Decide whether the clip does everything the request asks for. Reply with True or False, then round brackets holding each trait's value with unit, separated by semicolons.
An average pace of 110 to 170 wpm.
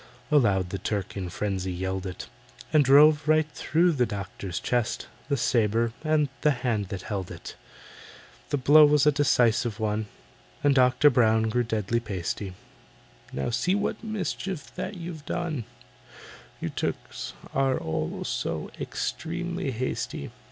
True (135 wpm)